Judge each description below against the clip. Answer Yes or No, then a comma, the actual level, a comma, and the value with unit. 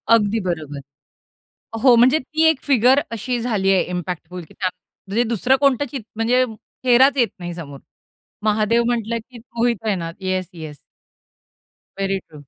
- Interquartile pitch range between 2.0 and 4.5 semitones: No, average, 5.0 semitones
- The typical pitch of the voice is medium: No, high, 225 Hz